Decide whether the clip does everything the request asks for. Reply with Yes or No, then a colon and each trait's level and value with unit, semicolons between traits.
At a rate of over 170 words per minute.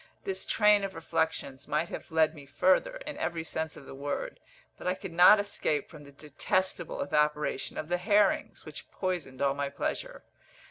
Yes: average, 180 wpm